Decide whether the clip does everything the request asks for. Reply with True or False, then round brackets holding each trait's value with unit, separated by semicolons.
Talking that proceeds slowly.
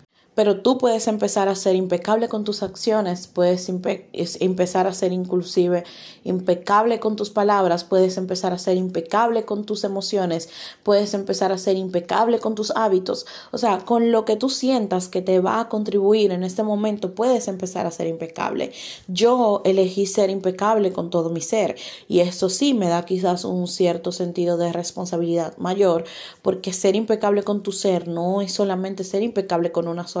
False (180 wpm)